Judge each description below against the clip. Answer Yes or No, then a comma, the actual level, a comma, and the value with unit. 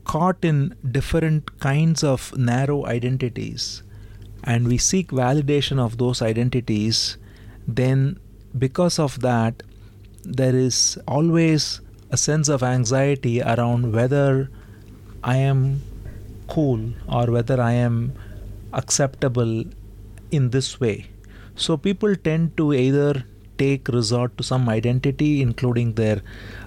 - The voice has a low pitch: Yes, low, 125 Hz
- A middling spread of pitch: Yes, average, 4.4 semitones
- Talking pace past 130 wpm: No, slow, 110 wpm